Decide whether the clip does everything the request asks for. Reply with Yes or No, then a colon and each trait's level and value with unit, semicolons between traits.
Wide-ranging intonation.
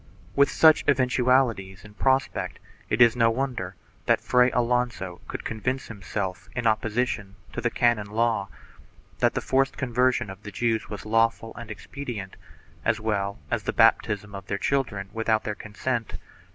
No: average, 3.4 semitones